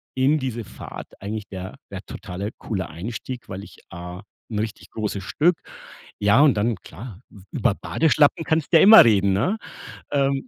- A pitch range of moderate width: No, wide, 6.2 semitones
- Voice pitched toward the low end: Yes, low, 110 Hz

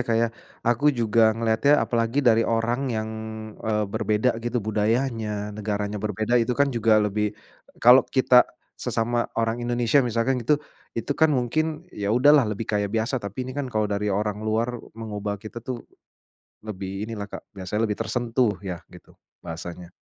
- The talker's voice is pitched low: Yes, low, 115 Hz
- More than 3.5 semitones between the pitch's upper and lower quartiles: No, narrow, 2.6 semitones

